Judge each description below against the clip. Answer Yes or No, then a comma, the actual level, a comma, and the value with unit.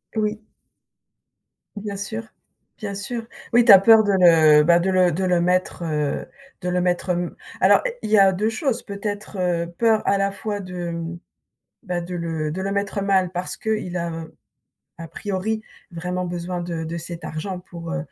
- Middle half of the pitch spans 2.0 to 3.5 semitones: Yes, average, 2.9 semitones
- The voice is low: No, medium, 185 Hz